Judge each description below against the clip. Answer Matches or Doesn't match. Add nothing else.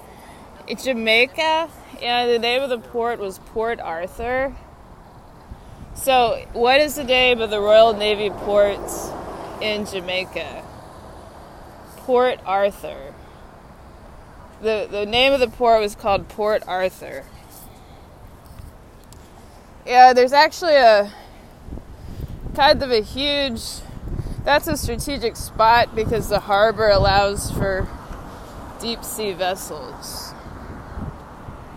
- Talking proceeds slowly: Matches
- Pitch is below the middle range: Doesn't match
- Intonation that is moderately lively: Matches